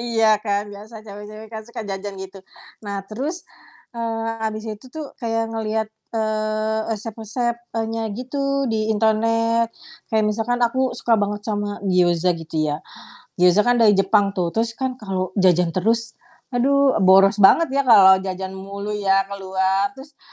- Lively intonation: No, average, 2.7 semitones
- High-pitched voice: Yes, high, 215 Hz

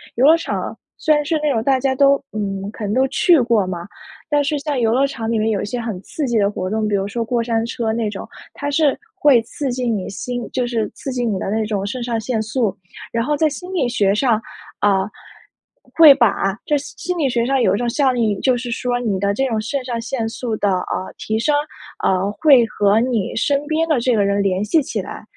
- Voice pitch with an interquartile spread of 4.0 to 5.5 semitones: Yes, average, 4.3 semitones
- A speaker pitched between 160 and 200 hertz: No, high, 235 Hz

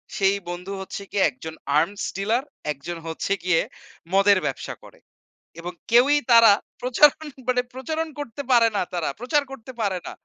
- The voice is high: Yes, high, 205 Hz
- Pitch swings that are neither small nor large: No, wide, 5.7 semitones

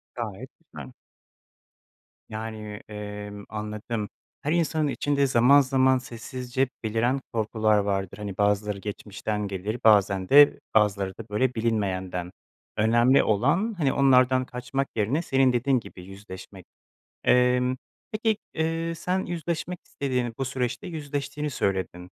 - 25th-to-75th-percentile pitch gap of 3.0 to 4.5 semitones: No, average, 4.9 semitones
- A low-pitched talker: Yes, low, 120 Hz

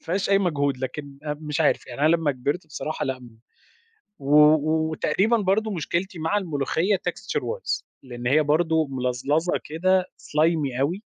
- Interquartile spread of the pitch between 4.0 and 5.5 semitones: Yes, average, 4.3 semitones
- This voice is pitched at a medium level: Yes, medium, 155 Hz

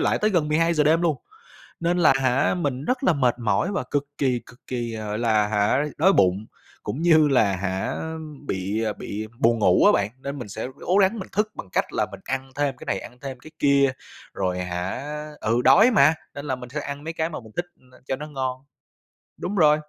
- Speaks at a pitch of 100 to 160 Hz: Yes, low, 135 Hz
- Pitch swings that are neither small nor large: No, wide, 5.9 semitones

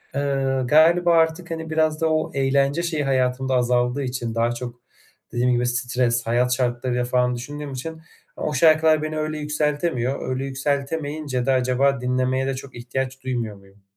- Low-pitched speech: Yes, low, 130 Hz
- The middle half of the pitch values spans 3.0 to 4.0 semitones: Yes, average, 3.4 semitones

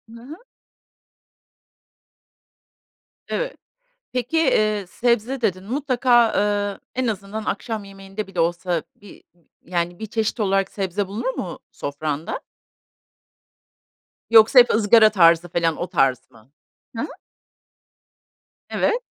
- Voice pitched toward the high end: Yes, high, 205 Hz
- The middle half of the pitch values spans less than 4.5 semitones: No, average, 4.8 semitones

